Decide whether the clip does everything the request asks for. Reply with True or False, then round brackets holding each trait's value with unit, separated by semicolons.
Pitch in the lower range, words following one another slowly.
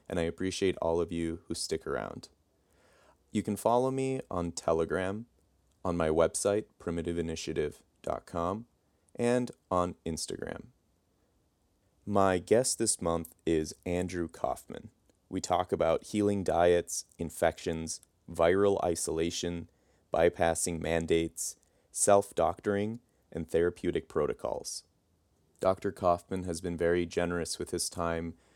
True (85 Hz; 110 wpm)